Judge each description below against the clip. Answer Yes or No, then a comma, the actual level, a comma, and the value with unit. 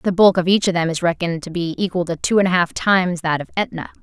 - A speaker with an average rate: No, fast, 300 wpm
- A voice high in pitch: No, medium, 180 Hz